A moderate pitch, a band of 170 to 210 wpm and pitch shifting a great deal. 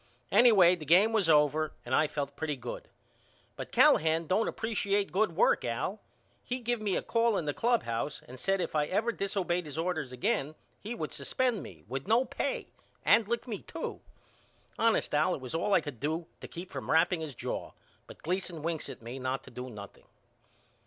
Yes: medium, 170 Hz; average, 195 wpm; wide, 5.9 semitones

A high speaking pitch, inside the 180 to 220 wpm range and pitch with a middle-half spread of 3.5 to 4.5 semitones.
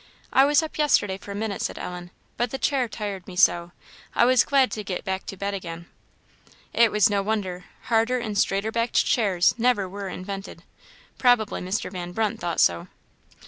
Yes: high, 205 Hz; average, 185 wpm; average, 3.9 semitones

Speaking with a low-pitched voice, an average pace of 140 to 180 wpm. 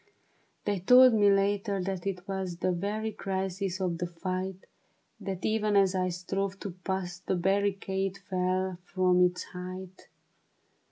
No: high, 190 Hz; average, 145 wpm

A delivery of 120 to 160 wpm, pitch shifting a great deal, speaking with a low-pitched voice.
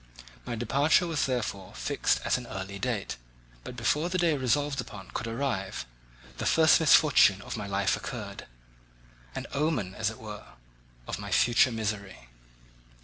Yes: average, 145 wpm; wide, 6.3 semitones; low, 110 Hz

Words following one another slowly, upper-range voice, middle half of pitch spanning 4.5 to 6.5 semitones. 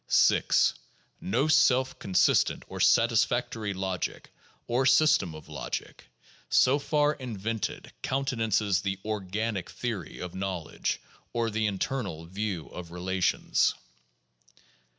No: slow, 105 wpm; low, 110 Hz; average, 5.0 semitones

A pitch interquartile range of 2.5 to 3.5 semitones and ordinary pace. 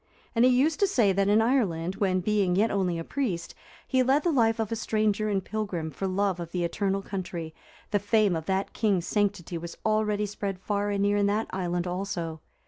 No: average, 3.2 semitones; fast, 215 wpm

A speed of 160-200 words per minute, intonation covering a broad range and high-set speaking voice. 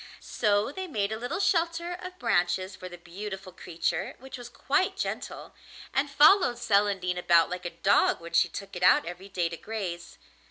Yes: average, 185 wpm; wide, 7.2 semitones; high, 200 Hz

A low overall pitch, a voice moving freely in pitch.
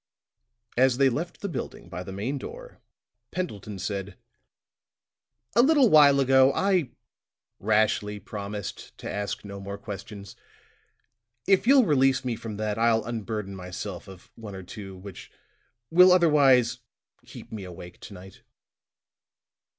Yes: low, 110 Hz; wide, 5.9 semitones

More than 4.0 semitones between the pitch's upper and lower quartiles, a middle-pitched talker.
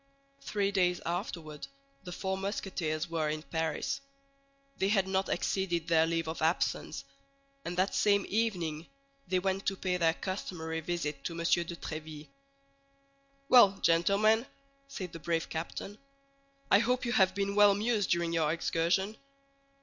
No: average, 3.3 semitones; medium, 180 Hz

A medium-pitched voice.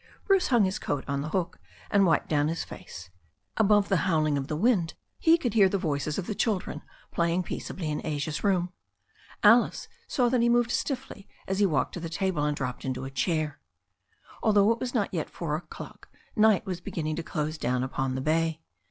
Yes: medium, 170 Hz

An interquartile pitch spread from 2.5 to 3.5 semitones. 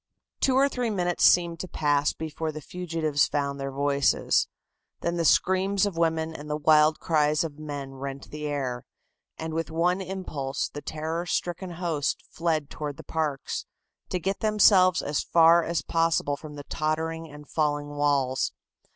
Yes: average, 2.8 semitones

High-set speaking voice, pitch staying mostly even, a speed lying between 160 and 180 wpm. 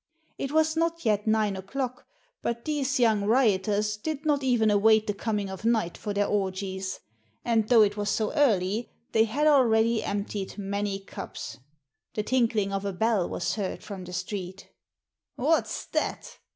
No: high, 215 Hz; average, 3.5 semitones; average, 165 wpm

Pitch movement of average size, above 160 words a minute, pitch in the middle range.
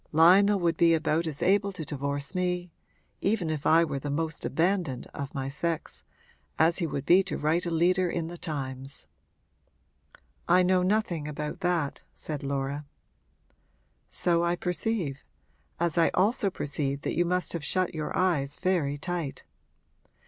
No: average, 3.7 semitones; average, 155 wpm; medium, 165 Hz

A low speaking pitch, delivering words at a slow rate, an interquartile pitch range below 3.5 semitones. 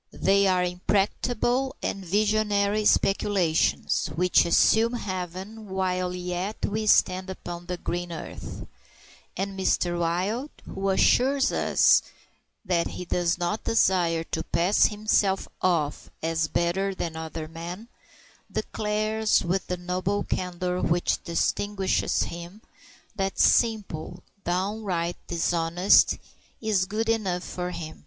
No: medium, 185 Hz; slow, 115 wpm; average, 3.0 semitones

